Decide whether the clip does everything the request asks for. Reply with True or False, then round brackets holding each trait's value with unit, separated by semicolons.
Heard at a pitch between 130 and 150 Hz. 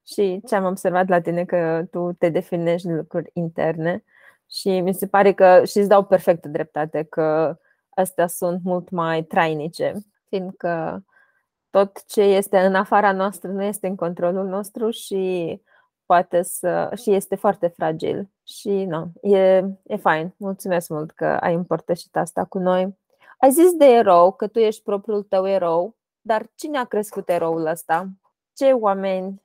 False (185 Hz)